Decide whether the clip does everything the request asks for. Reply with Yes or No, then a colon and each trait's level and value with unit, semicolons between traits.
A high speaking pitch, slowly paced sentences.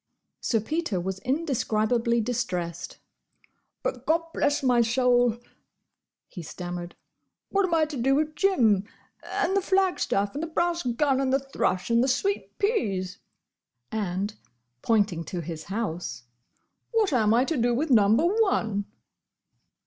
Yes: high, 240 Hz; slow, 125 wpm